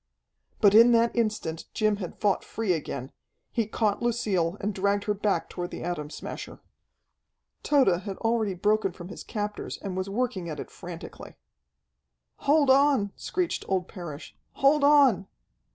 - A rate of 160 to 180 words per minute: No, average, 150 wpm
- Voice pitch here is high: Yes, high, 205 Hz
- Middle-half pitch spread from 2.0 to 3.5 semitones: No, average, 4.3 semitones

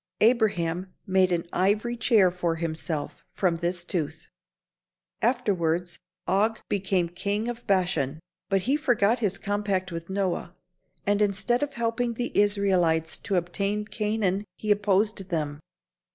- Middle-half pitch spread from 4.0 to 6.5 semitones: No, average, 3.4 semitones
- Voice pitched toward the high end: Yes, high, 195 Hz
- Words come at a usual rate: No, slow, 130 wpm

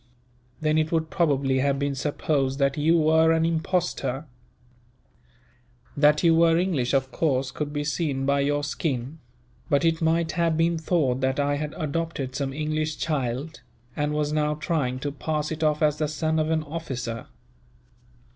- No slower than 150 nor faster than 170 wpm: Yes, average, 165 wpm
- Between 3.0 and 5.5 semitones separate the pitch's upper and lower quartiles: No, narrow, 2.5 semitones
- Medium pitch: Yes, medium, 150 Hz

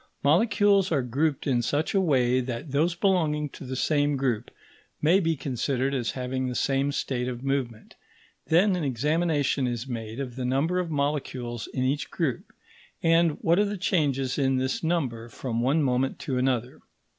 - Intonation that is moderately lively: Yes, average, 4.1 semitones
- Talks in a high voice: No, low, 135 Hz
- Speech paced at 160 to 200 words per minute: Yes, average, 175 wpm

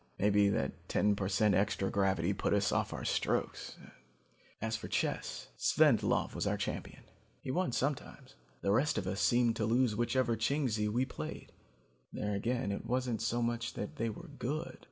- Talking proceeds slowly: No, average, 175 wpm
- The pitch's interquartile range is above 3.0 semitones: Yes, average, 3.6 semitones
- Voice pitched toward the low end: Yes, low, 110 Hz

